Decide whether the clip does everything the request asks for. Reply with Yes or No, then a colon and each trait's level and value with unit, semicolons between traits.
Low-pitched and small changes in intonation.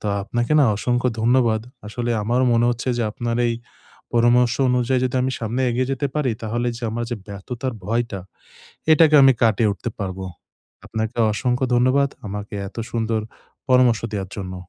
Yes: low, 120 Hz; narrow, 2.3 semitones